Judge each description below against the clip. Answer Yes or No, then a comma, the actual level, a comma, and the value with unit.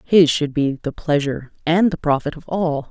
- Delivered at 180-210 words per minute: Yes, fast, 205 wpm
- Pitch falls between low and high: Yes, medium, 155 Hz